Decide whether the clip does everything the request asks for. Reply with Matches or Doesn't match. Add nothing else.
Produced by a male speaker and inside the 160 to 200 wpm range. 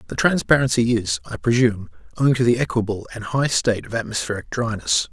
Matches